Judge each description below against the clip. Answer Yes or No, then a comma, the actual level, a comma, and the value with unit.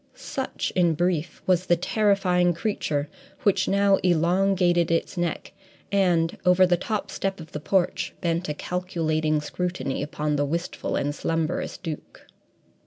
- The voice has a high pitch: No, medium, 175 Hz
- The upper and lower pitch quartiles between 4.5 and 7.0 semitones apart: No, average, 2.7 semitones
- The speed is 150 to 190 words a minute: No, average, 140 wpm